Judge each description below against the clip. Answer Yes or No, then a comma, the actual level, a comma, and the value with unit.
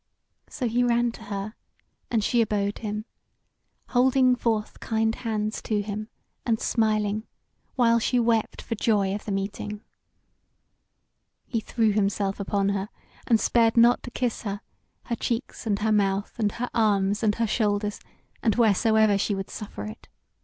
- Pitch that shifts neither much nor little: No, narrow, 2.2 semitones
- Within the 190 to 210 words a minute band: No, average, 155 wpm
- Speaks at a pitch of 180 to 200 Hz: No, high, 215 Hz